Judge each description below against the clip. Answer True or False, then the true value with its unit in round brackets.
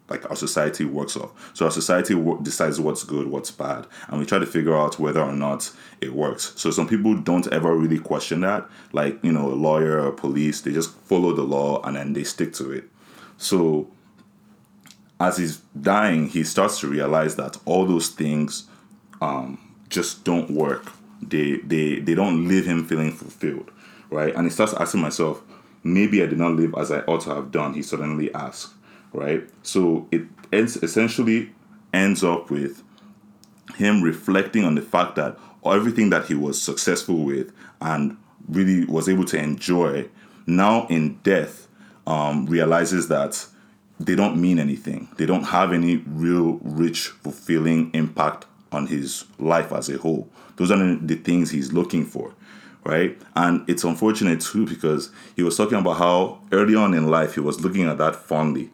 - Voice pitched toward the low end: True (80 Hz)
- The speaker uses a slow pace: False (175 wpm)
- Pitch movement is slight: False (3.0 semitones)